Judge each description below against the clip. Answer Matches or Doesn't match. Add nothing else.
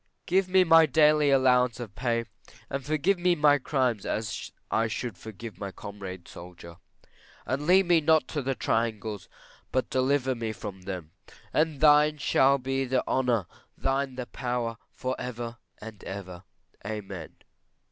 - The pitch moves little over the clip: Doesn't match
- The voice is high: Doesn't match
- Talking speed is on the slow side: Doesn't match